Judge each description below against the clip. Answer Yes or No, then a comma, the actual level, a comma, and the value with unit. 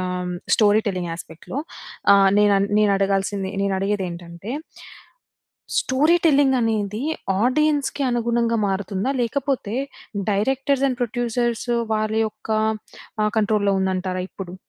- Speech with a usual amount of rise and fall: Yes, average, 4.0 semitones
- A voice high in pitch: Yes, high, 210 Hz